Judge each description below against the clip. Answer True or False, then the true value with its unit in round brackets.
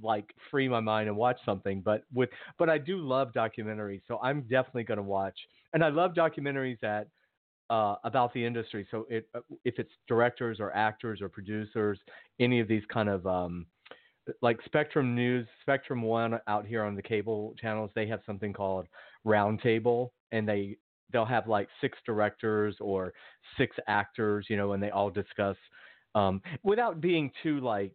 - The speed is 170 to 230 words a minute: True (175 wpm)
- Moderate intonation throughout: True (3.1 semitones)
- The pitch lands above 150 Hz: False (110 Hz)